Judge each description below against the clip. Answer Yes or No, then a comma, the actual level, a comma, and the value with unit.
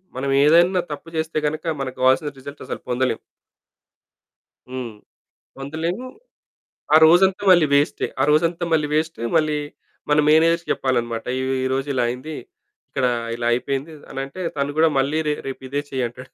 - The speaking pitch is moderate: Yes, medium, 145 Hz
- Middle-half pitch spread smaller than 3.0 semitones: No, average, 3.6 semitones